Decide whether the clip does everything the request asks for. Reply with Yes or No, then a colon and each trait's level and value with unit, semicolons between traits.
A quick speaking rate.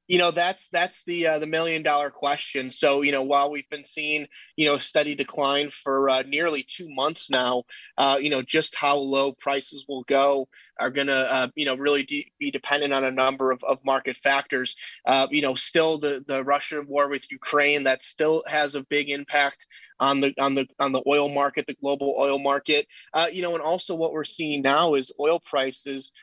Yes: fast, 215 wpm